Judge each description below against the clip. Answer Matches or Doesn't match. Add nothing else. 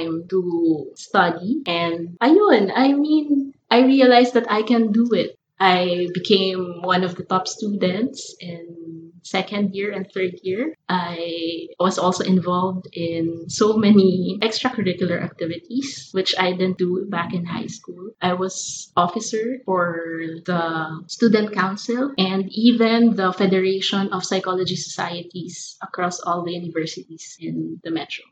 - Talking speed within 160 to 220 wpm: Doesn't match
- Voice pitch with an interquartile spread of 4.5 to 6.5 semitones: Doesn't match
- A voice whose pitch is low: Doesn't match